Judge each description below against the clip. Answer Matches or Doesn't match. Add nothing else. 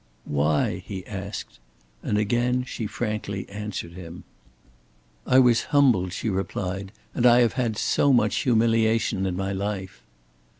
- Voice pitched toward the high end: Doesn't match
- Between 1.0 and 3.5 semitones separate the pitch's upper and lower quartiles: Doesn't match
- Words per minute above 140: Doesn't match